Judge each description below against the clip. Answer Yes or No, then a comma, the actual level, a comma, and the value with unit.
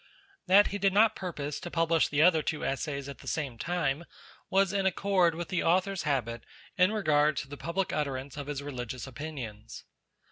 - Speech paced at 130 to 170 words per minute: No, average, 185 wpm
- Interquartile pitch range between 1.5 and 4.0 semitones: No, average, 4.7 semitones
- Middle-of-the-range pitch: Yes, medium, 155 Hz